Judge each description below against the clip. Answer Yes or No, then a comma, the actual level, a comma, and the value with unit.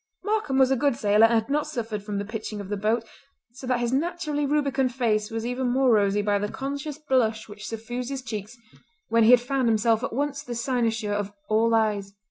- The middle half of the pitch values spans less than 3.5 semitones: No, average, 3.8 semitones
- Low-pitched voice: No, high, 235 Hz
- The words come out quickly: Yes, fast, 220 wpm